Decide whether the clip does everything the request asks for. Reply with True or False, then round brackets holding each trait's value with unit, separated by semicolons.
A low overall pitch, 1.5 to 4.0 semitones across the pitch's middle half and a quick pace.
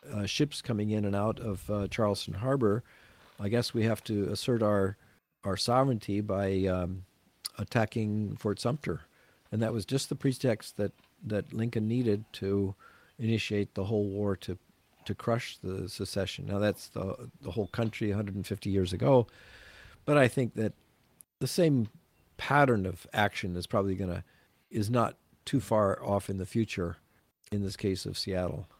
False (105 Hz; 2.8 semitones; 165 wpm)